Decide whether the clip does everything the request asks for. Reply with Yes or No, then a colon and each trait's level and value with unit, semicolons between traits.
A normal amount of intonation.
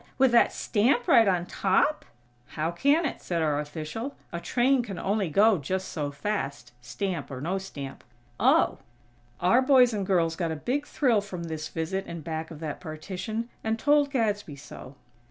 No: wide, 6.5 semitones